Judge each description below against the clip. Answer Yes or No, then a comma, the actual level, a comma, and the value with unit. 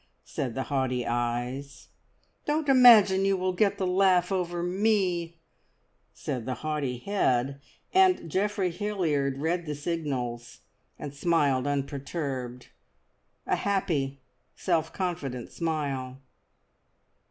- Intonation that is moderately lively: No, wide, 5.7 semitones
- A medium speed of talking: No, slow, 110 wpm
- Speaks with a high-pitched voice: No, medium, 155 Hz